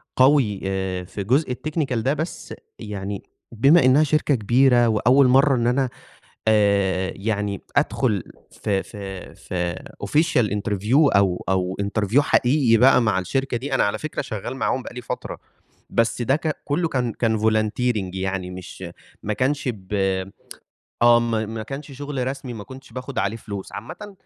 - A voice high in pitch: No, low, 115 Hz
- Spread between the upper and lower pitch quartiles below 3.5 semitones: No, average, 4.9 semitones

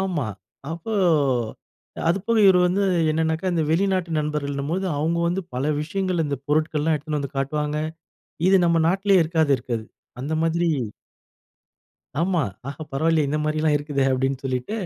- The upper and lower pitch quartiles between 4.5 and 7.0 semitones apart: No, average, 3.4 semitones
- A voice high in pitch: No, medium, 160 Hz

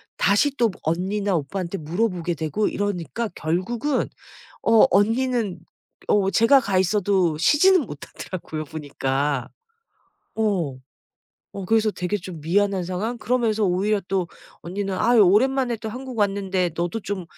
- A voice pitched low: No, high, 200 Hz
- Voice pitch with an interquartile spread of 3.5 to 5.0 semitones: Yes, average, 4.2 semitones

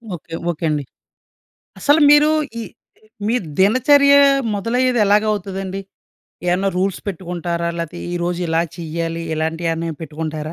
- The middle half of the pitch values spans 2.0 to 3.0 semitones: No, average, 3.8 semitones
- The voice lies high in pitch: No, medium, 175 Hz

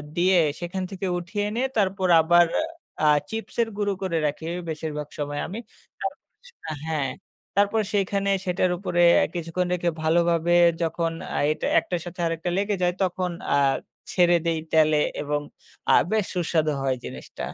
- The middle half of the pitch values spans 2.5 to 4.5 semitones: Yes, average, 3.0 semitones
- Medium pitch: Yes, medium, 175 Hz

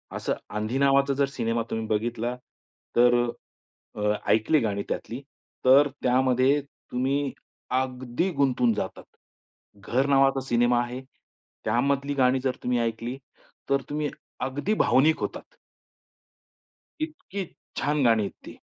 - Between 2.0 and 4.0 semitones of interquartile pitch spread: Yes, average, 2.8 semitones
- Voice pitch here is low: Yes, low, 130 Hz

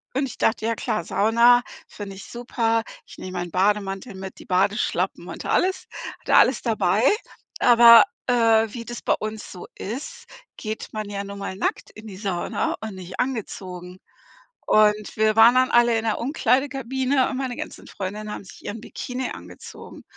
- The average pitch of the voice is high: Yes, high, 220 Hz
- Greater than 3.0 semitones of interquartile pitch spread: Yes, average, 3.5 semitones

